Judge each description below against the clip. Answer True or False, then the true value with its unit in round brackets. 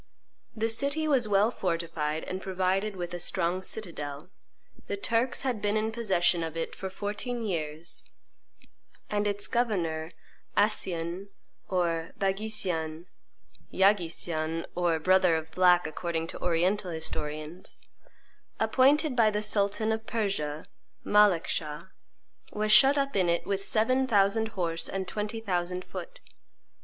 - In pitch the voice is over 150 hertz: True (190 Hz)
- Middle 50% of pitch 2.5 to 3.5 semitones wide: False (4.3 semitones)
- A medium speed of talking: False (130 wpm)